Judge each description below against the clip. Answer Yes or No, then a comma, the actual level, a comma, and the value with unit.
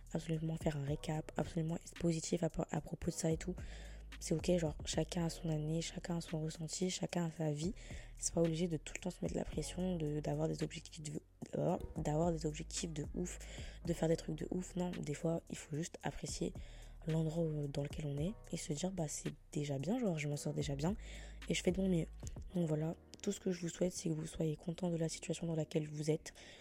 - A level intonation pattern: Yes, narrow, 1.9 semitones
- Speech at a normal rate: No, fast, 245 wpm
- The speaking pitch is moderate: Yes, medium, 165 Hz